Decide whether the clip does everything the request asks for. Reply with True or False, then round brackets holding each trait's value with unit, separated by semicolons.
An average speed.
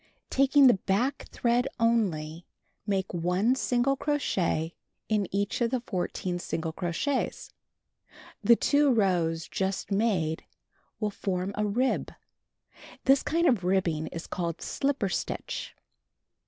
False (120 wpm)